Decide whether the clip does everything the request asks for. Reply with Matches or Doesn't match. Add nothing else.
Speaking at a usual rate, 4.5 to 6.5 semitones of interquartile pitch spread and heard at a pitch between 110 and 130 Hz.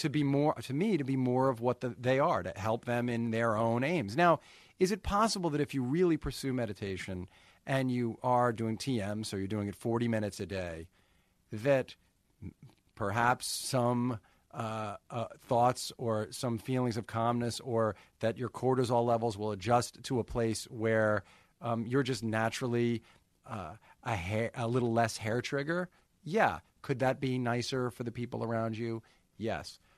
Doesn't match